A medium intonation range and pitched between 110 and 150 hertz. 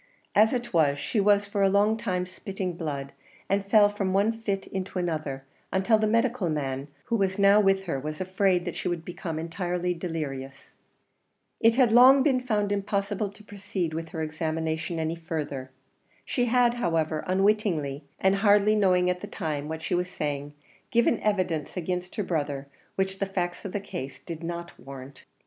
No: average, 4.3 semitones; medium, 185 Hz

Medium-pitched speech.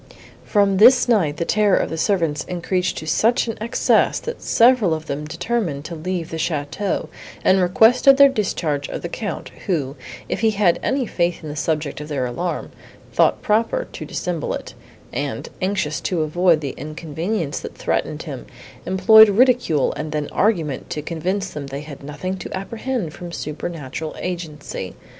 Yes: medium, 175 Hz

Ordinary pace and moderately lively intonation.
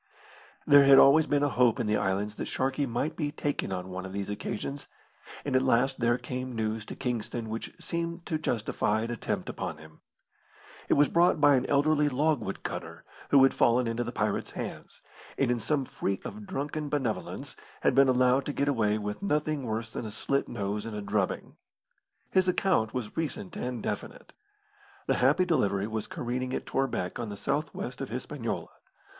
Yes: average, 190 wpm; average, 4.8 semitones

